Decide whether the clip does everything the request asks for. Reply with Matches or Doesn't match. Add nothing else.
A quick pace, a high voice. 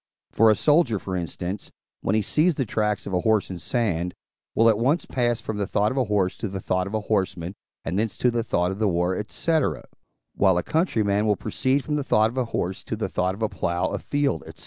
Doesn't match